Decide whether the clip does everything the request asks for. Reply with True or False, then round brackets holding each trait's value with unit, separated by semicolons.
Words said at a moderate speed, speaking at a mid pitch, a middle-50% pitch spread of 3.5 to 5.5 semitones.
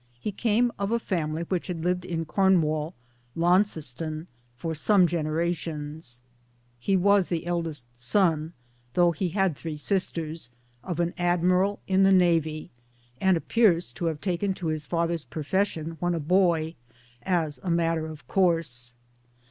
False (145 wpm; 170 Hz; 2.9 semitones)